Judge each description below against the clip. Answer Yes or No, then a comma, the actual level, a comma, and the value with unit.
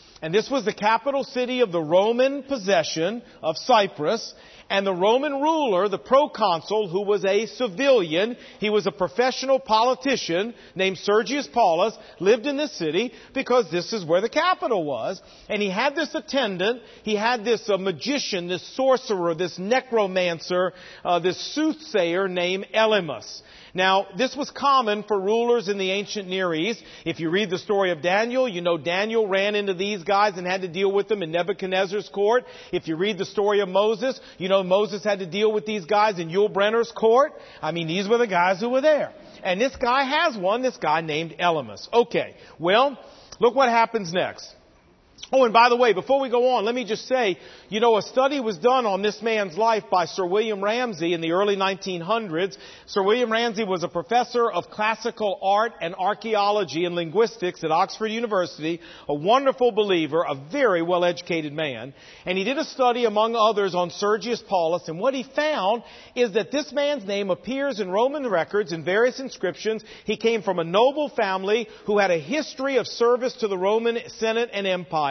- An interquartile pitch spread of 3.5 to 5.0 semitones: Yes, average, 4.7 semitones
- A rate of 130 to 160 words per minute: No, average, 190 wpm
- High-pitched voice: Yes, high, 210 Hz